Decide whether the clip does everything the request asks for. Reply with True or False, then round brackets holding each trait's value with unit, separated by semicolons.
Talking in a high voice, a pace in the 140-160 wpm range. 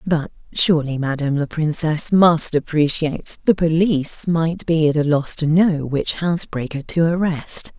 False (160 Hz; 155 wpm)